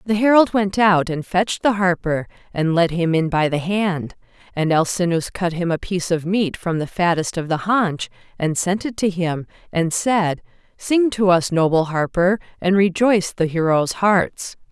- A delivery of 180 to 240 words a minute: Yes, average, 190 wpm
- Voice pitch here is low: No, medium, 180 Hz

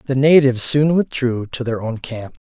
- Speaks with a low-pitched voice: Yes, low, 130 Hz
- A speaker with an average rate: Yes, average, 195 wpm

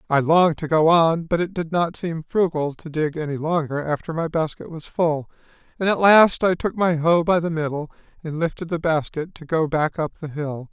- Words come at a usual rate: No, fast, 225 wpm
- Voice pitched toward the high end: No, medium, 160 Hz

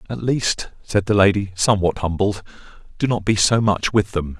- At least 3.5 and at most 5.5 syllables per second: Yes, 5.1 syllables/s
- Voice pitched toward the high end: No, low, 100 Hz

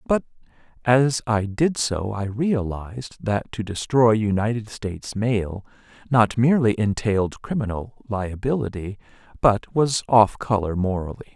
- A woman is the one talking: No, male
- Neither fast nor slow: No, slow, 120 wpm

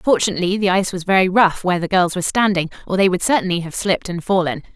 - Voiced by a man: No, female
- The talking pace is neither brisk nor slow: No, fast, 240 wpm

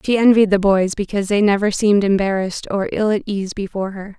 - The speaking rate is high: Yes, fast, 215 wpm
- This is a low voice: No, high, 200 Hz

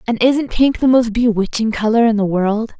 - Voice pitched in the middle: No, high, 225 Hz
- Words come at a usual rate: No, fast, 215 wpm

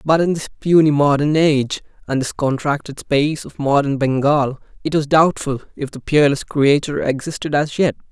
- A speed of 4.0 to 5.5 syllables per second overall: Yes, 5.2 syllables/s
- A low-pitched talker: No, medium, 145 Hz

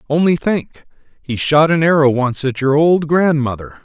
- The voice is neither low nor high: Yes, medium, 145 Hz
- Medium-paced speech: Yes, average, 170 wpm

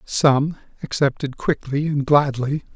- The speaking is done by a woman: No, male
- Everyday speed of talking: No, slow, 110 wpm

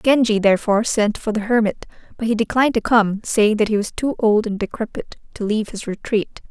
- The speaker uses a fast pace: Yes, fast, 210 wpm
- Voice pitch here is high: Yes, high, 220 Hz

